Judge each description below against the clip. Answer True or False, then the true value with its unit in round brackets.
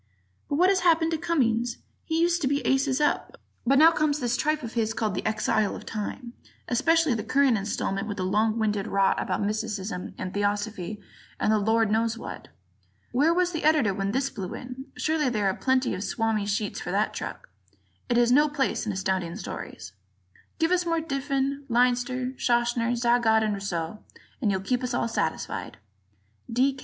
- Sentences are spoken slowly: False (190 wpm)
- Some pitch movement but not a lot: True (4.8 semitones)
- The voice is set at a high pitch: True (240 Hz)